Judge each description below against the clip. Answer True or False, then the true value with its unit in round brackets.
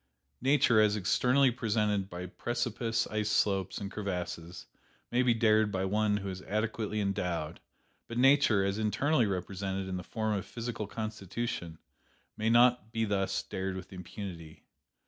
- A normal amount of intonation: True (3.1 semitones)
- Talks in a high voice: False (105 Hz)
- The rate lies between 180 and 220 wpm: False (145 wpm)